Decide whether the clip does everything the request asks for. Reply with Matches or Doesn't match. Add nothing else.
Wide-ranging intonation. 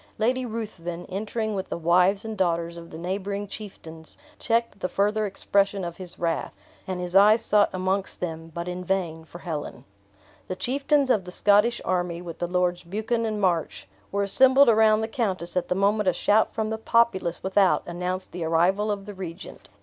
Doesn't match